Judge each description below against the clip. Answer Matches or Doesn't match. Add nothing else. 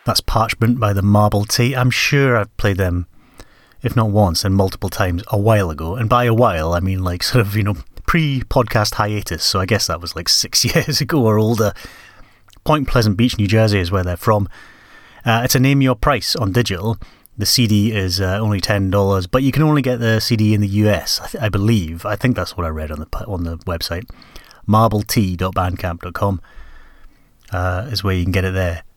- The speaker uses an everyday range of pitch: Matches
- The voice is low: Matches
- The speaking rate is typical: Doesn't match